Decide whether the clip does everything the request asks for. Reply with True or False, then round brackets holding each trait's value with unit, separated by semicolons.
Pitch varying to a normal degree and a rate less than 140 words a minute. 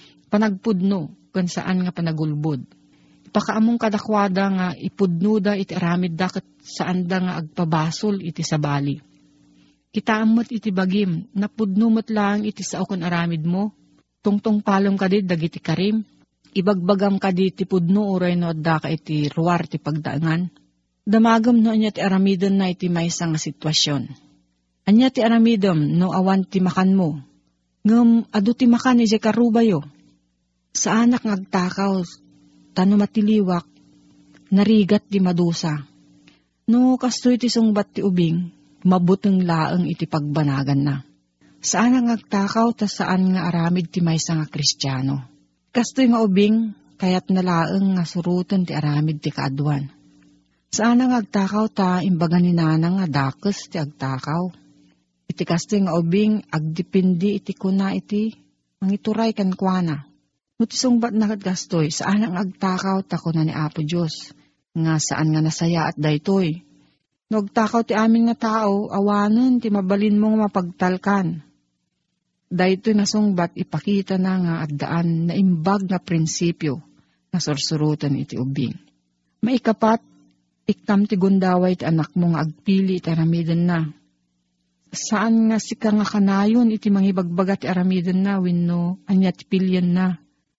True (4.4 semitones; 130 wpm)